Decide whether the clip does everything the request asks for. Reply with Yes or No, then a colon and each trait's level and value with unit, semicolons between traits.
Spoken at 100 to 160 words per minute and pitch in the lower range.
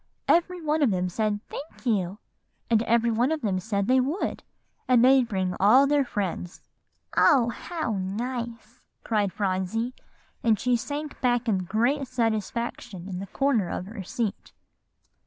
No: average, 155 wpm; high, 230 Hz